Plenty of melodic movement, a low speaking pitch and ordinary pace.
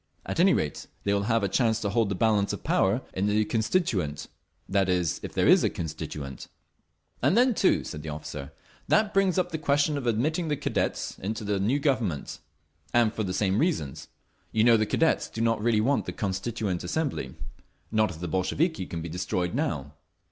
Yes: wide, 7.1 semitones; low, 110 Hz; average, 190 wpm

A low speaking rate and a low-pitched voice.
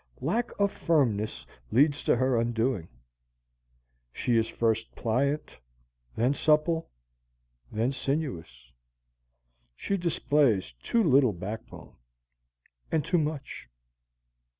Yes: slow, 95 wpm; low, 130 Hz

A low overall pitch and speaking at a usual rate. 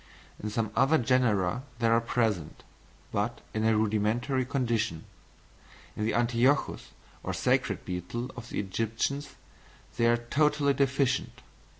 No: low, 115 Hz; slow, 125 wpm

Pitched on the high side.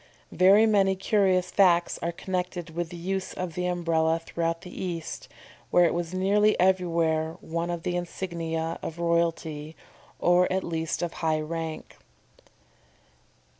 No: medium, 170 Hz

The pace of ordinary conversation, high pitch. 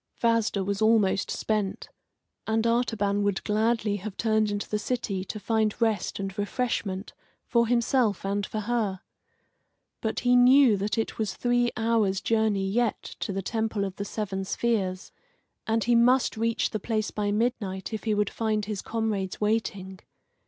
Yes: average, 160 wpm; high, 215 Hz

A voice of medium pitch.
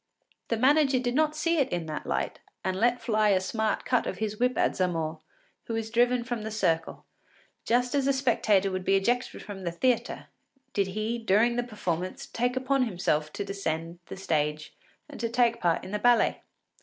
No: high, 220 Hz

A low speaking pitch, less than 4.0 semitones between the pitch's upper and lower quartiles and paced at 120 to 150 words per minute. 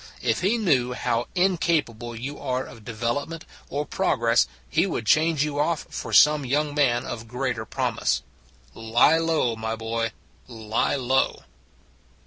No: low, 125 Hz; average, 4.7 semitones; average, 140 wpm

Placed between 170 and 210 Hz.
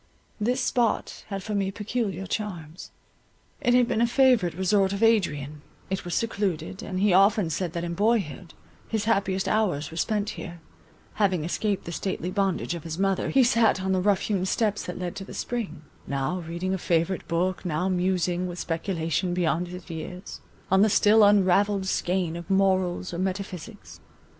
Yes: high, 190 Hz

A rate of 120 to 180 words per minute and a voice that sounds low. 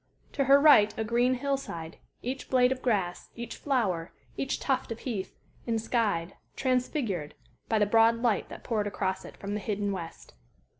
No: average, 170 wpm; high, 225 Hz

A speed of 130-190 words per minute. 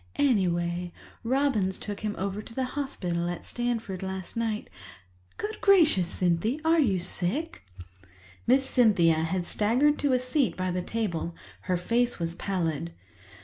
Yes: average, 140 wpm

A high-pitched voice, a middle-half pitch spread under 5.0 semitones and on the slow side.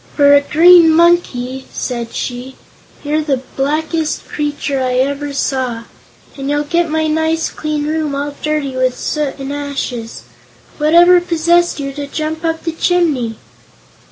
No: very high, 290 Hz; average, 2.8 semitones; average, 145 wpm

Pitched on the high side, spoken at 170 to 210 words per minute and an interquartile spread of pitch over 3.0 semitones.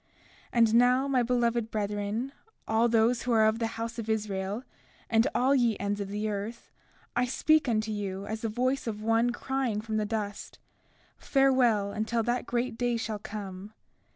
No: high, 225 Hz; average, 180 wpm; narrow, 2.4 semitones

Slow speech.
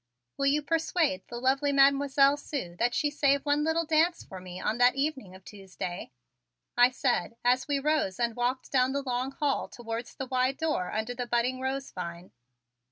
No: average, 185 wpm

